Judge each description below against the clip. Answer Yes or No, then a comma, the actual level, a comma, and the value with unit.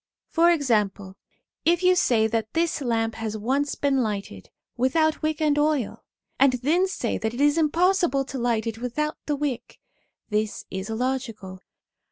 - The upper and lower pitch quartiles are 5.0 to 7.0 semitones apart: Yes, wide, 5.4 semitones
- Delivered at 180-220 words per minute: No, average, 160 wpm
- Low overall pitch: No, very high, 260 Hz